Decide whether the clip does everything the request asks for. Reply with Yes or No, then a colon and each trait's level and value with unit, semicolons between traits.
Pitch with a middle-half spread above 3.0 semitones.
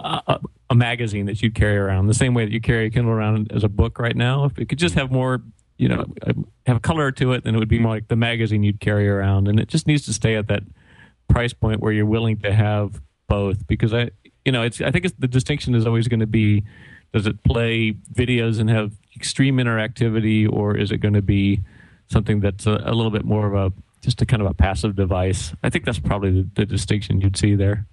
No: narrow, 2.5 semitones